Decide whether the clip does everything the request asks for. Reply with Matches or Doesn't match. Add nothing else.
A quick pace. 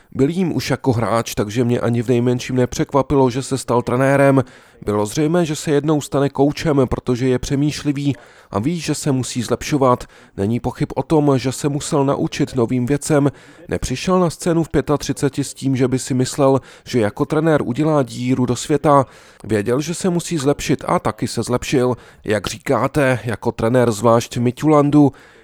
Matches